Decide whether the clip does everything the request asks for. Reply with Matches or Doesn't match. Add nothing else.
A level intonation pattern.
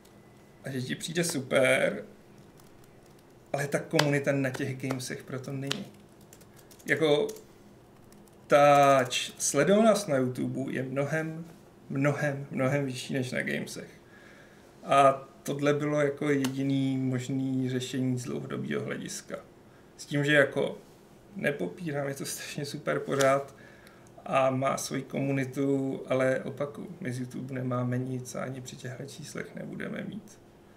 Matches